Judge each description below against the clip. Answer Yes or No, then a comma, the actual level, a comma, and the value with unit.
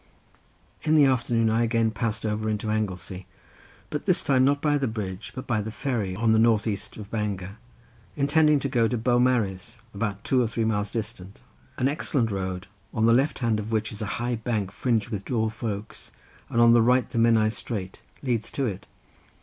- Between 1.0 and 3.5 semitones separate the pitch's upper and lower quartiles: Yes, narrow, 2.6 semitones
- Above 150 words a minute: Yes, average, 200 wpm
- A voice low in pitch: Yes, low, 110 Hz